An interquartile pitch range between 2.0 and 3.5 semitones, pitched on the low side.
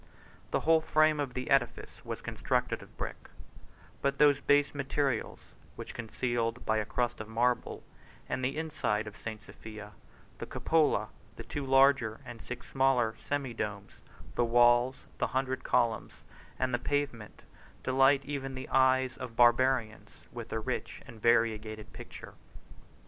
Yes: average, 3.0 semitones; low, 125 Hz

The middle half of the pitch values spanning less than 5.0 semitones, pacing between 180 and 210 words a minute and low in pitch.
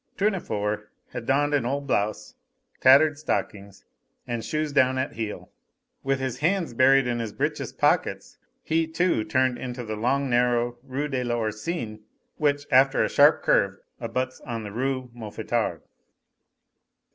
No: average, 3.6 semitones; average, 145 wpm; low, 130 Hz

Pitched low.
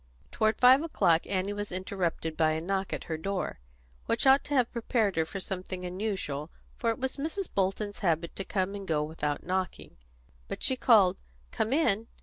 No: high, 195 Hz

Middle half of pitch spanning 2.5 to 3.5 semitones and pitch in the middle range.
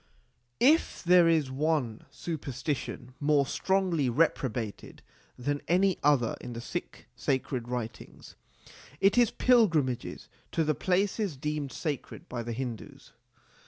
No: average, 5.2 semitones; medium, 145 Hz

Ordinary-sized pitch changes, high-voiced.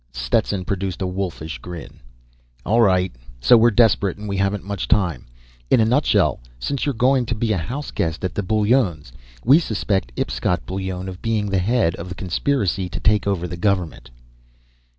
No: average, 3.8 semitones; low, 100 Hz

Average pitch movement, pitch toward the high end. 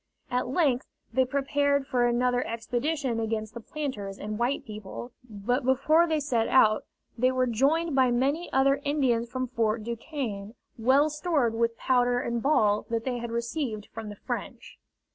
Yes: average, 3.3 semitones; high, 245 Hz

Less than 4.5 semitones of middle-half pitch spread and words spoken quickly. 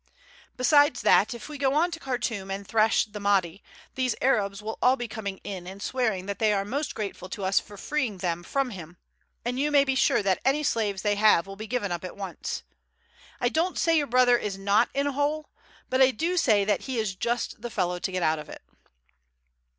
No: average, 5.1 semitones; fast, 225 wpm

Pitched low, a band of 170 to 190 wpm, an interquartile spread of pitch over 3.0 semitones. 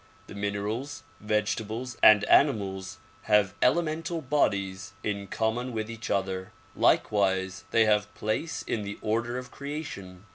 No: low, 105 Hz; slow, 135 wpm; average, 3.8 semitones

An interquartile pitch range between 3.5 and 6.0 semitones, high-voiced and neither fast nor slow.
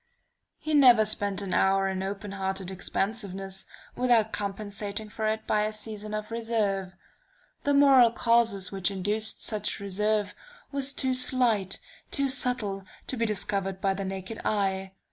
No: average, 3.0 semitones; high, 210 Hz; average, 145 wpm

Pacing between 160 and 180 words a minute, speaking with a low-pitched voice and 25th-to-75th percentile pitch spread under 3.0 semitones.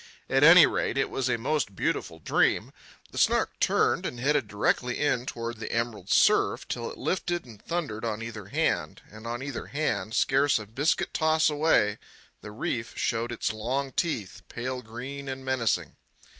No: average, 170 wpm; low, 120 Hz; average, 4.0 semitones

